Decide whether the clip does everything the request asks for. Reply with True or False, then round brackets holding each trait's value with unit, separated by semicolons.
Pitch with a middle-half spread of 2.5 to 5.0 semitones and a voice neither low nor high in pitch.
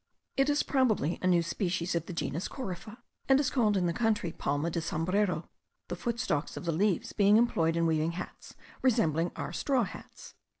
False (5.5 semitones; 180 Hz)